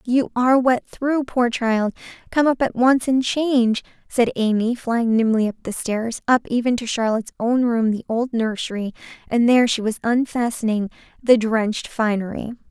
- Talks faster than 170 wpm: No, average, 165 wpm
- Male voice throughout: No, female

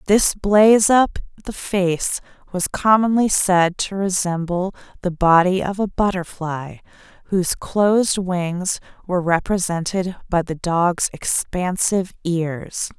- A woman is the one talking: Yes, female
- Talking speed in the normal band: No, slow, 115 wpm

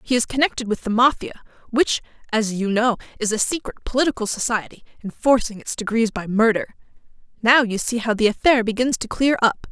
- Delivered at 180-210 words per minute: Yes, average, 185 wpm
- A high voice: Yes, high, 230 Hz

